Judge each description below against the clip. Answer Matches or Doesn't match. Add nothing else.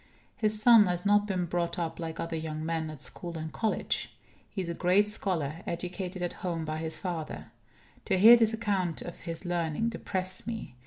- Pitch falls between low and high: Matches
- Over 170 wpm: Matches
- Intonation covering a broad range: Doesn't match